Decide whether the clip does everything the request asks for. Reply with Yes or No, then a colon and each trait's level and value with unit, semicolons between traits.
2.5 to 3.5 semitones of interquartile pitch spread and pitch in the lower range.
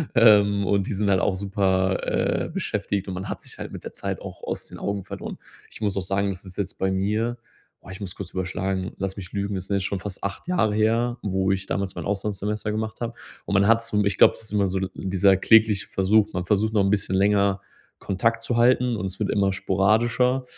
No: narrow, 2.0 semitones; low, 100 Hz